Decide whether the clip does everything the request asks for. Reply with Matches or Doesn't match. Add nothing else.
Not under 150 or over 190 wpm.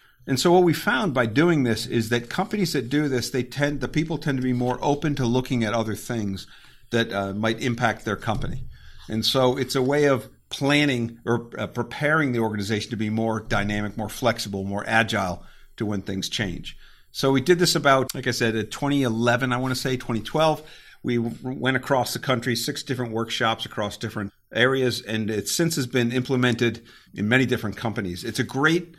Doesn't match